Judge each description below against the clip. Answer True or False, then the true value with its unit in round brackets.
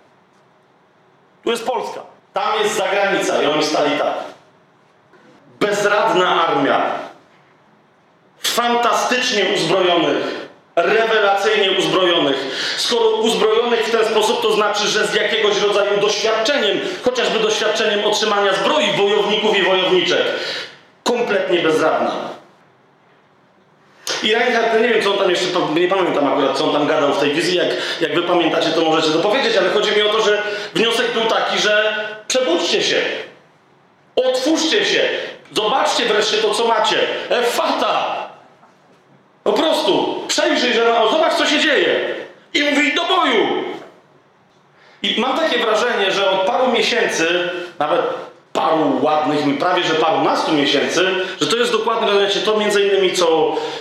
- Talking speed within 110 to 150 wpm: True (135 wpm)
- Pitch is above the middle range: True (215 Hz)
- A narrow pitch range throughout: False (4.9 semitones)